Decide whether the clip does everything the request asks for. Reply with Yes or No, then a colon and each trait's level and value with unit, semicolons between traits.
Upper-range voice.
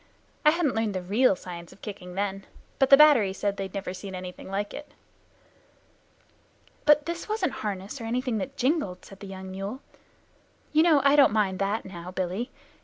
Yes: high, 205 Hz